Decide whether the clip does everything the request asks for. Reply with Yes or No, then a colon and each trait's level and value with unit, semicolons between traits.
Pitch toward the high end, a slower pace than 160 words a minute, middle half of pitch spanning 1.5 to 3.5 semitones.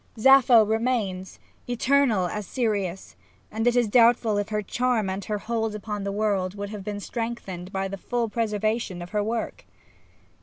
No: high, 215 Hz; average, 165 wpm; average, 2.8 semitones